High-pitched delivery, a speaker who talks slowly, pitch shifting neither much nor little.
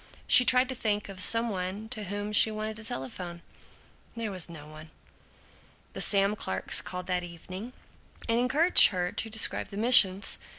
No: high, 205 Hz; average, 170 wpm; average, 3.7 semitones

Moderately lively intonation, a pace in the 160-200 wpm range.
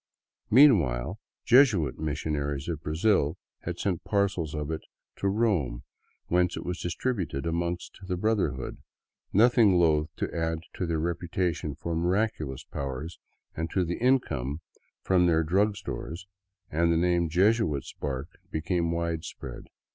No: average, 3.6 semitones; average, 140 wpm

